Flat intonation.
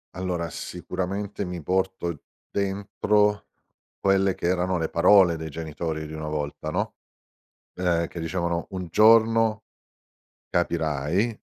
No: average, 3.0 semitones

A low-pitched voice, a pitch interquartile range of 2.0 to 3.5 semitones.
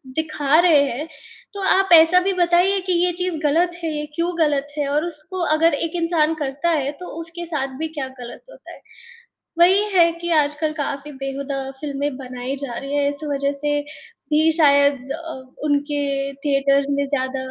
No: very high, 295 Hz; average, 3.1 semitones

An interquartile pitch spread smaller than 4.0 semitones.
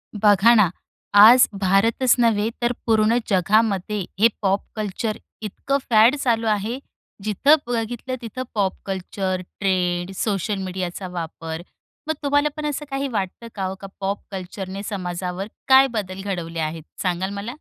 Yes: average, 3.5 semitones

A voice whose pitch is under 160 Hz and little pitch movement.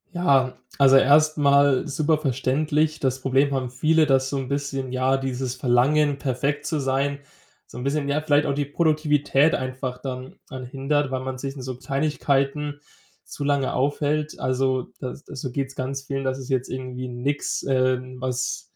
Yes: low, 135 Hz; narrow, 2.0 semitones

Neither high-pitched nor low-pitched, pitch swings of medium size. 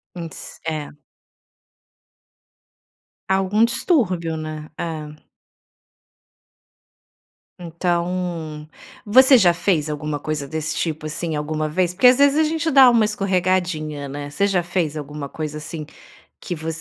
Yes: medium, 170 Hz; average, 4.0 semitones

